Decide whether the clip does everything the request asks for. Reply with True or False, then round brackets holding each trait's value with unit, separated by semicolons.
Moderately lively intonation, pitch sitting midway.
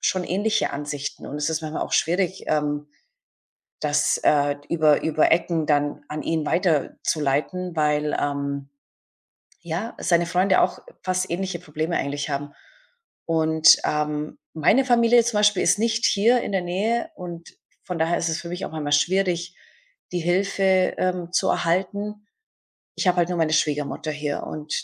True (3.7 semitones; 170 Hz)